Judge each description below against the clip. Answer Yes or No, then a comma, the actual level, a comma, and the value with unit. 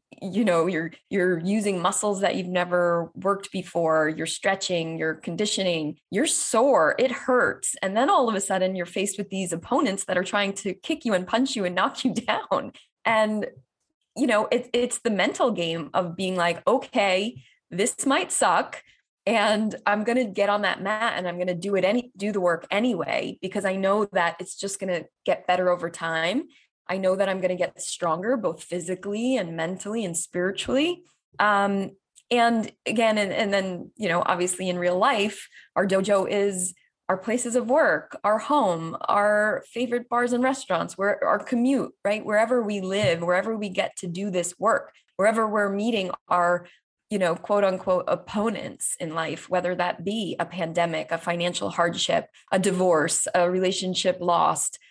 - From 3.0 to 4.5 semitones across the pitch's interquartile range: Yes, average, 3.6 semitones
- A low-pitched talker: No, high, 195 Hz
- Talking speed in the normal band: Yes, average, 185 wpm